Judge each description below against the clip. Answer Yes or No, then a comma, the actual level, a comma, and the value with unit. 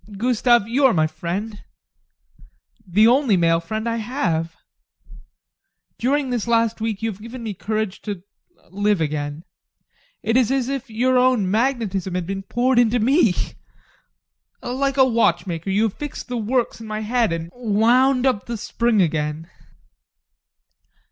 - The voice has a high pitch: Yes, high, 220 Hz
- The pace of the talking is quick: No, average, 150 wpm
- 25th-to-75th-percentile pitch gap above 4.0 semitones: Yes, average, 4.5 semitones